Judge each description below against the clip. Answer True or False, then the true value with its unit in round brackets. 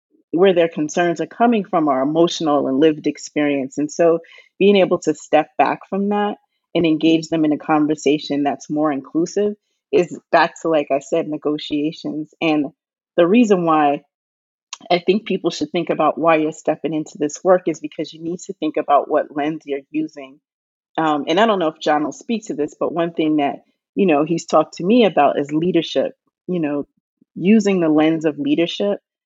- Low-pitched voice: False (160 Hz)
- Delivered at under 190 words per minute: False (195 wpm)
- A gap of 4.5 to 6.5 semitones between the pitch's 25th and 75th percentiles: False (3.2 semitones)